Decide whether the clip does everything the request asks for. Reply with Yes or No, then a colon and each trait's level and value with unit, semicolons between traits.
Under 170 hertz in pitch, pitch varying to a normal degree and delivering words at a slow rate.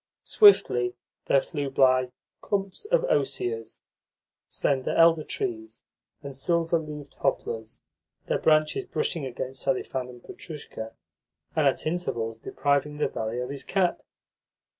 Yes: medium, 140 Hz; average, 4.7 semitones; slow, 120 wpm